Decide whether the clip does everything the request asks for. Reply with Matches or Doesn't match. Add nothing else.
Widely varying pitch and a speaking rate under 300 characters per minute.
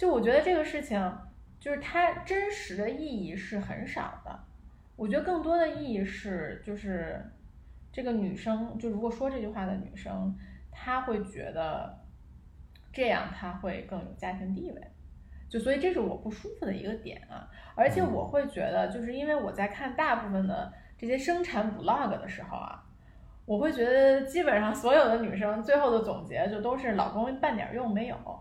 Matches